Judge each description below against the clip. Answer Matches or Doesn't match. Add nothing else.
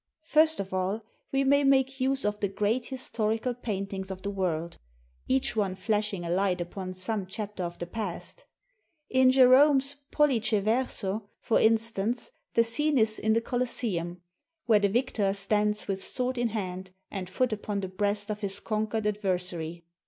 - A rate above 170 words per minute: Doesn't match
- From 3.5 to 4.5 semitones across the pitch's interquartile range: Matches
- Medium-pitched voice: Doesn't match